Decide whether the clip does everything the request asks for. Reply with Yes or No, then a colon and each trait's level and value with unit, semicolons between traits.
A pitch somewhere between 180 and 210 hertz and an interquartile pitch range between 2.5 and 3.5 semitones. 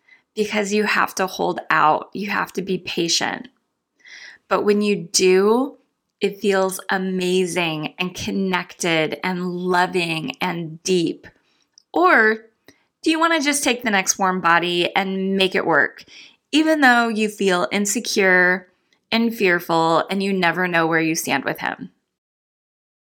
Yes: high, 190 Hz; average, 2.9 semitones